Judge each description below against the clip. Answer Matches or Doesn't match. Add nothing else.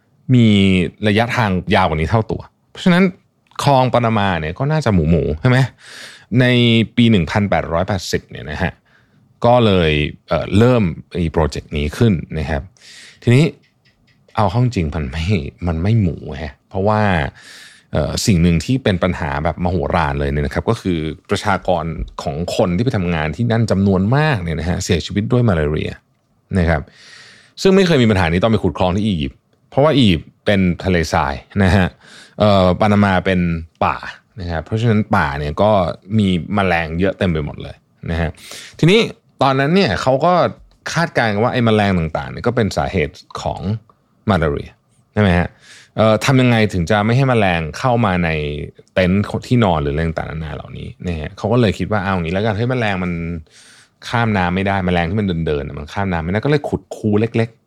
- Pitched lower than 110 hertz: Matches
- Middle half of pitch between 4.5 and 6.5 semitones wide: Matches